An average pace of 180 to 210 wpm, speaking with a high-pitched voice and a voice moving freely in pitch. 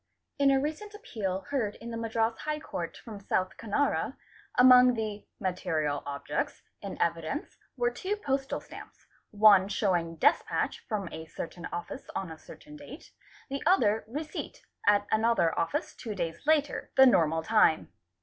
No: average, 150 wpm; high, 220 Hz; wide, 6.8 semitones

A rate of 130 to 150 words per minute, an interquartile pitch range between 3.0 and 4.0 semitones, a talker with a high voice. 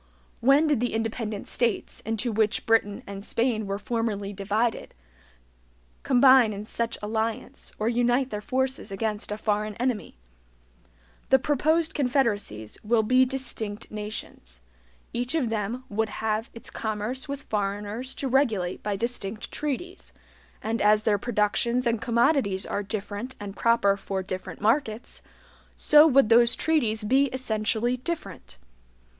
Yes: slow, 135 wpm; average, 3.4 semitones; high, 225 Hz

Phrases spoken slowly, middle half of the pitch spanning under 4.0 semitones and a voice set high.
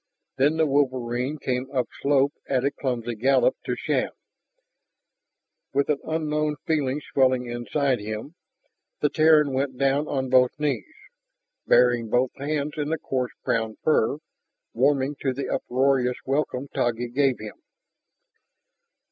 No: slow, 130 wpm; average, 2.7 semitones; low, 135 Hz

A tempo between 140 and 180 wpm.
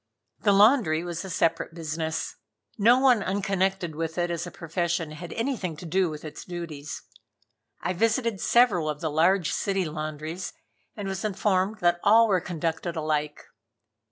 Yes: average, 155 wpm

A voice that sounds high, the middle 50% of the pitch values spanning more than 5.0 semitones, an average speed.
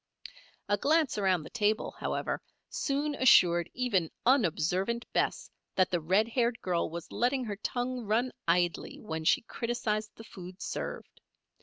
Yes: high, 215 Hz; wide, 5.4 semitones; average, 145 wpm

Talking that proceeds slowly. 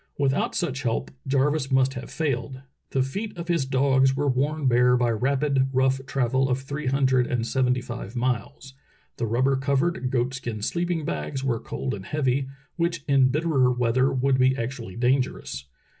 No: average, 175 wpm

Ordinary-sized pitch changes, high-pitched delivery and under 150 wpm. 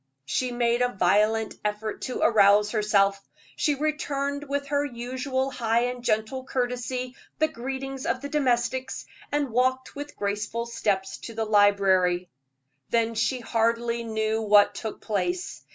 Yes: average, 3.6 semitones; high, 235 Hz; average, 140 wpm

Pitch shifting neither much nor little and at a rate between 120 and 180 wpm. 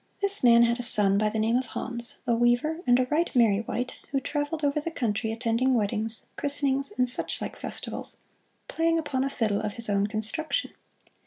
No: average, 4.1 semitones; average, 195 wpm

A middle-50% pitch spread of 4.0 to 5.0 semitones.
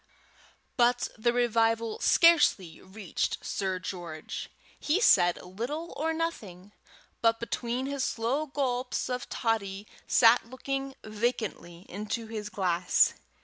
Yes: average, 4.7 semitones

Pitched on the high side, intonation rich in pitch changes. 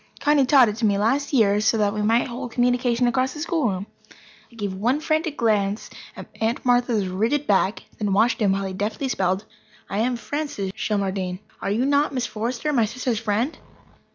No: high, 230 Hz; average, 4.0 semitones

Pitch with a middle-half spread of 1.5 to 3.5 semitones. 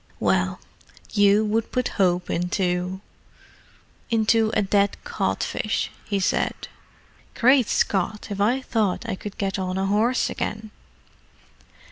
Yes: narrow, 2.6 semitones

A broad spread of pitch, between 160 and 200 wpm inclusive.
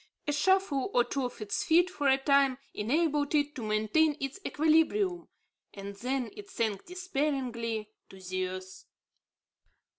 No: wide, 6.4 semitones; average, 145 wpm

